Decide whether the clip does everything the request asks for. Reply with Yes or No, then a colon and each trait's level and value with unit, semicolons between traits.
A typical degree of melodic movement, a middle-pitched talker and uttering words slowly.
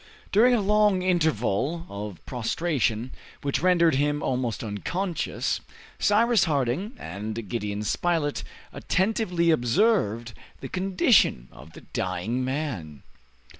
No: wide, 8.6 semitones; medium, 145 Hz; slow, 105 wpm